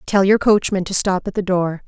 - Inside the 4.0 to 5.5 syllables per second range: Yes, 5.2 syllables/s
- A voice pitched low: No, high, 190 Hz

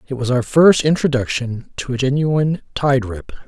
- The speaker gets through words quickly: No, average, 175 wpm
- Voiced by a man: Yes, male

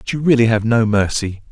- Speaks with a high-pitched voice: No, low, 115 Hz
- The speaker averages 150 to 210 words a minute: No, fast, 240 wpm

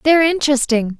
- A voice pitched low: No, very high, 275 Hz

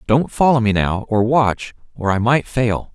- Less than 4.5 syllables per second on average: Yes, 4.3 syllables/s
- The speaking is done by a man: Yes, male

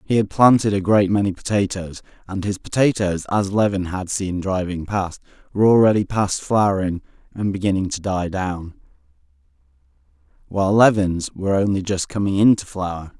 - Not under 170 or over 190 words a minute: No, average, 150 wpm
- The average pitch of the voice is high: No, very low, 95 Hz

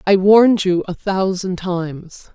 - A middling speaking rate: Yes, average, 155 wpm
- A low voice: No, medium, 185 Hz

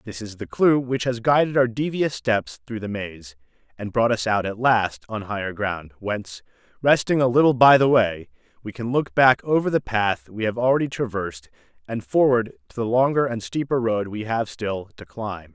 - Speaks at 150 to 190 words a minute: No, fast, 205 wpm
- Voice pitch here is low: Yes, low, 115 Hz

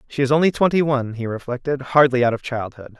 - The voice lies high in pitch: No, low, 130 Hz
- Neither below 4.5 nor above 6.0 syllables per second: No, 6.4 syllables/s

